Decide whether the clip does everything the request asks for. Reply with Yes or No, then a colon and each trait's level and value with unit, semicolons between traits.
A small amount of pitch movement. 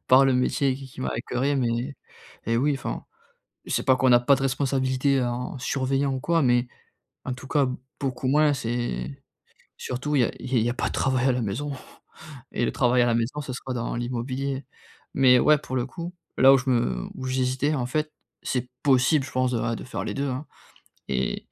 Yes: narrow, 2.0 semitones